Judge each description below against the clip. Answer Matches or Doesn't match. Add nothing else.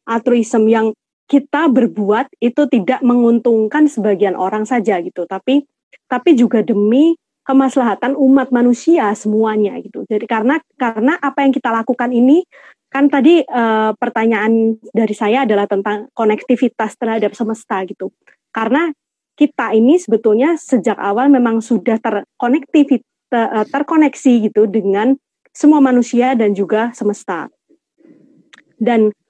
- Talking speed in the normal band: Matches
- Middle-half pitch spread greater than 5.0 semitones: Doesn't match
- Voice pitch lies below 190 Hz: Doesn't match